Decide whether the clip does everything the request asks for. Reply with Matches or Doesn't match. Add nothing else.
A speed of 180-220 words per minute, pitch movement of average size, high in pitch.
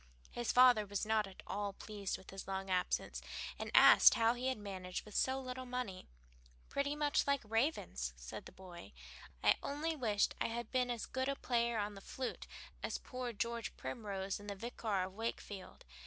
Matches